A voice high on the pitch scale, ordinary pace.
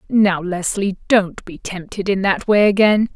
Yes: high, 195 Hz; average, 170 wpm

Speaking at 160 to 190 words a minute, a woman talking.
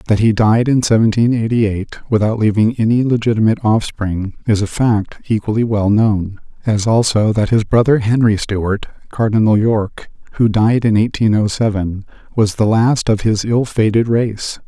No: average, 170 wpm; male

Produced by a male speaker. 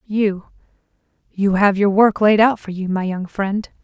No: female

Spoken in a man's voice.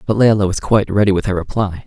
Yes: male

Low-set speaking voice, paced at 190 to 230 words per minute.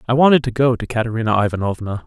Yes: low, 115 Hz; fast, 205 wpm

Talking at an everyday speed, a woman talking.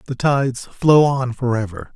No: average, 155 wpm; male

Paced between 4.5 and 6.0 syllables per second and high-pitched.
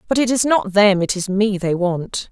Yes: 4.7 syllables/s; high, 200 Hz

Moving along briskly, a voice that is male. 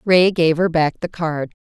No: fast, 220 wpm; female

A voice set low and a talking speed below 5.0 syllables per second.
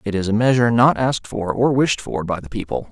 No: low, 110 Hz; 6.1 syllables/s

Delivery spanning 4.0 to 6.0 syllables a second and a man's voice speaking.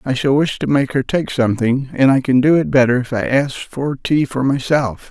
Yes: 5.0 syllables/s; male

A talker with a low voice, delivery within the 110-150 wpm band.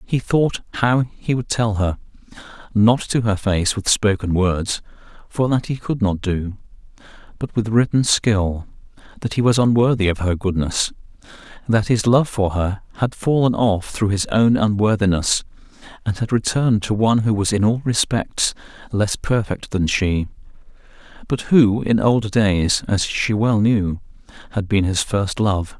No: low, 105 Hz; average, 160 wpm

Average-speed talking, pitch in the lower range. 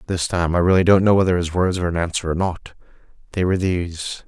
No: fast, 240 wpm; very low, 90 Hz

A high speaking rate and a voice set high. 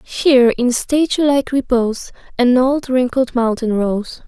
No: average, 140 wpm; very high, 255 Hz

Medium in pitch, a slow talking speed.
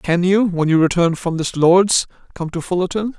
No: medium, 175 Hz; fast, 205 wpm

